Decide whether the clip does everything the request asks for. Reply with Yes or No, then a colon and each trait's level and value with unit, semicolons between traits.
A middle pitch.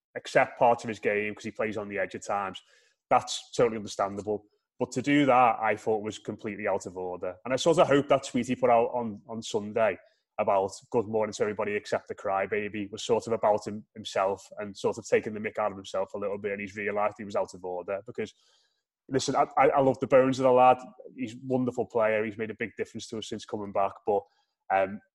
No: low, 110 Hz